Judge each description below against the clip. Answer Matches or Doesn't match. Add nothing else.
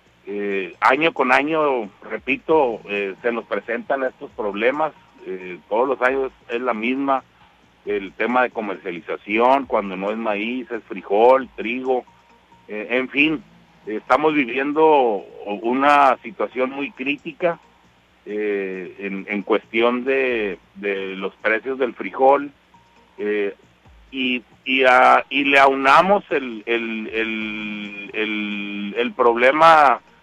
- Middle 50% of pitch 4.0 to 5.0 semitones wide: Matches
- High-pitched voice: Doesn't match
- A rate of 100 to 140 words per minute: Matches